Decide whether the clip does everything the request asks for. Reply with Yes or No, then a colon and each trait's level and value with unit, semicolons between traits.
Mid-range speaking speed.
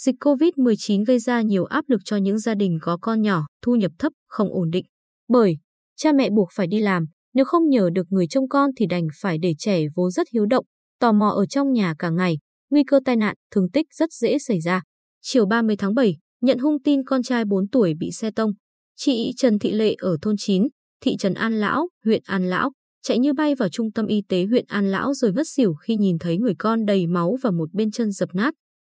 Yes: average, 240 wpm